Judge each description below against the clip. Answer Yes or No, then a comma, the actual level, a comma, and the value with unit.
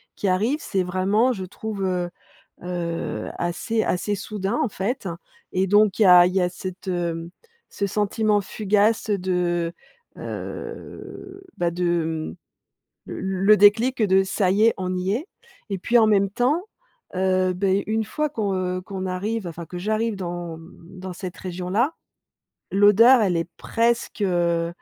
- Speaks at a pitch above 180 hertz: Yes, high, 190 Hz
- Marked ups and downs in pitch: No, average, 3.1 semitones